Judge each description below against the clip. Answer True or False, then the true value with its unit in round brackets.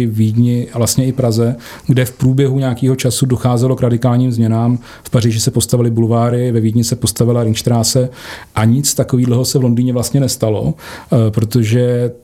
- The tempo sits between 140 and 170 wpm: True (165 wpm)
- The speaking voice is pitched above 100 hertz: True (120 Hz)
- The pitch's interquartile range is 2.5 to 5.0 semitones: False (1.5 semitones)